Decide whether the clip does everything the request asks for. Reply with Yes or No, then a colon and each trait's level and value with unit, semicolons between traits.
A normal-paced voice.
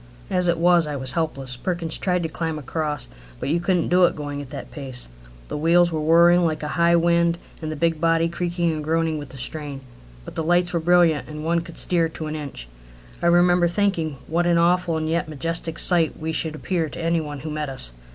No: fast, 230 wpm